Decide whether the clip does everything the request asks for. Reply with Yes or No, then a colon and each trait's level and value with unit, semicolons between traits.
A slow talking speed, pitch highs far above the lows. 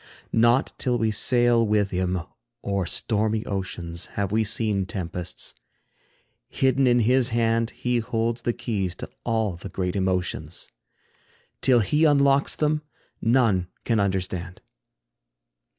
No: slow, 125 wpm; average, 4.3 semitones